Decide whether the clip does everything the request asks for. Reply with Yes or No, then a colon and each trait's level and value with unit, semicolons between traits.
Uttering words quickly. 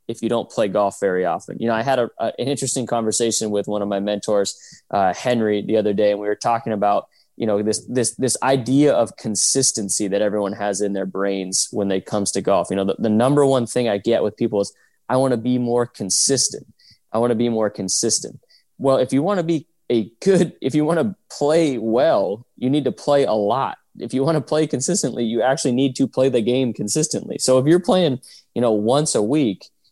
Yes: fast, 235 wpm